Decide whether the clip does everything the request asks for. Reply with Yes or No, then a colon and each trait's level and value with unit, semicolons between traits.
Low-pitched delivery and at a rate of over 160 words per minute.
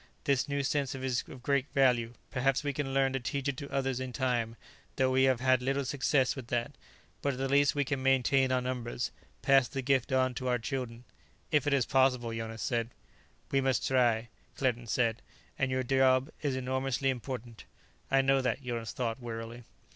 Yes: low, 130 Hz; average, 200 wpm